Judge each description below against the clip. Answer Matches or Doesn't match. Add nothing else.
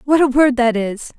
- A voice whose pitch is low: Doesn't match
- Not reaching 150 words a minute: Doesn't match